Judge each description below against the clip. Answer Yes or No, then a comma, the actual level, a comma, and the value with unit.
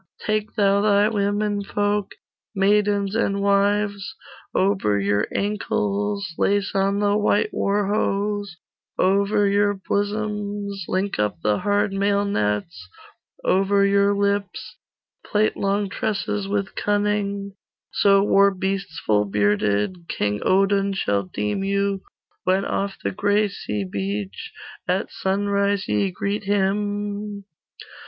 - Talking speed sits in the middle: No, slow, 115 wpm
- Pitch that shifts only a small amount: Yes, narrow, 1.1 semitones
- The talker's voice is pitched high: Yes, high, 200 Hz